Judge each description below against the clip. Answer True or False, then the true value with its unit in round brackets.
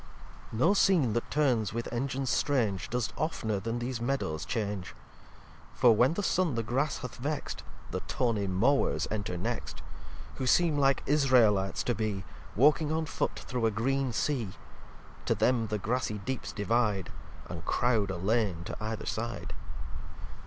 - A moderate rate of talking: True (155 wpm)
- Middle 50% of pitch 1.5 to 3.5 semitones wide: False (4.3 semitones)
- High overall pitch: False (120 Hz)